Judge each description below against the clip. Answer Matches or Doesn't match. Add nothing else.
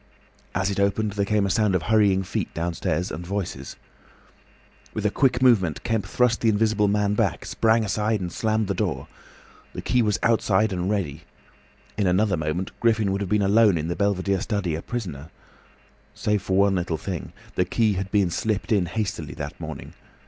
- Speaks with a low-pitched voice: Matches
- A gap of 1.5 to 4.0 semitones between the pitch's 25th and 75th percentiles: Matches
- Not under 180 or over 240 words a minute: Matches